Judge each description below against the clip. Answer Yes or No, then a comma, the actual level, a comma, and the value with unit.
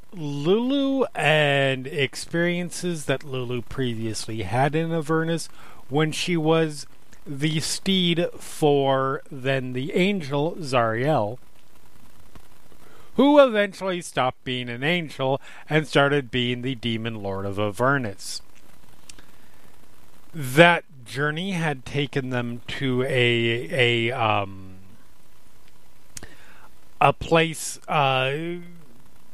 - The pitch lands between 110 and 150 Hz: Yes, medium, 140 Hz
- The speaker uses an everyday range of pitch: Yes, average, 4.7 semitones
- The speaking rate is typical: No, slow, 90 wpm